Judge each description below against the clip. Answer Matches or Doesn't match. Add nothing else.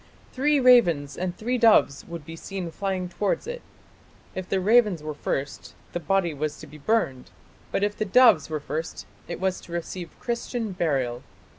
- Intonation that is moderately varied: Doesn't match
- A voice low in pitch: Doesn't match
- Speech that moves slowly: Doesn't match